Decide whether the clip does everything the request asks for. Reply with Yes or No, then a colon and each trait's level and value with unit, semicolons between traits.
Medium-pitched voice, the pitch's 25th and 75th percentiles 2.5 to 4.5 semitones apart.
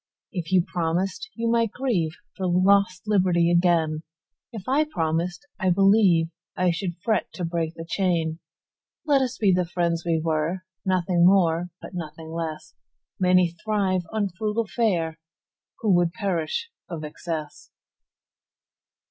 Yes: medium, 180 Hz; average, 3.1 semitones